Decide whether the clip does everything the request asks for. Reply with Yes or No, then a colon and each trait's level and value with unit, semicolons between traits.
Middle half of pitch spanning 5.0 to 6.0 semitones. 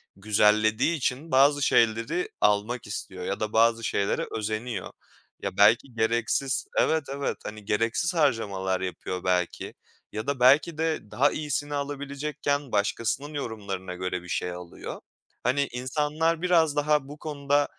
Yes: wide, 5.6 semitones